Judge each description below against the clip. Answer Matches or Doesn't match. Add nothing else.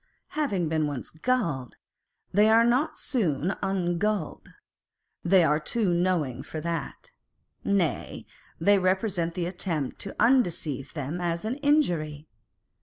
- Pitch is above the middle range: Doesn't match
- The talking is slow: Matches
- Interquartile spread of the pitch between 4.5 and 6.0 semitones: Matches